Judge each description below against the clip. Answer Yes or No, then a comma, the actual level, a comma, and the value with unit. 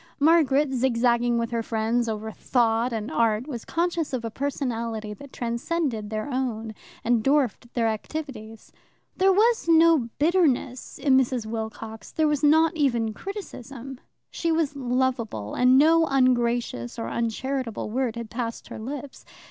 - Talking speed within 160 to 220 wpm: No, average, 145 wpm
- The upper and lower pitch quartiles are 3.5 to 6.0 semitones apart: Yes, average, 4.0 semitones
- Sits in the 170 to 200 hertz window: No, high, 245 Hz